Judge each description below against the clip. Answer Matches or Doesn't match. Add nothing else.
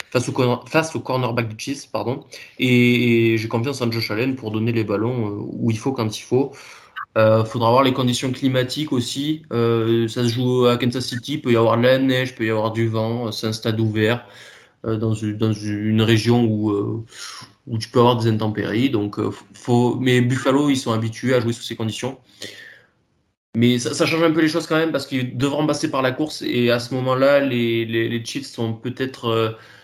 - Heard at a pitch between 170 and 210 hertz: Doesn't match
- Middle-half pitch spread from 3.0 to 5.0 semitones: Doesn't match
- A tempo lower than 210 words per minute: Doesn't match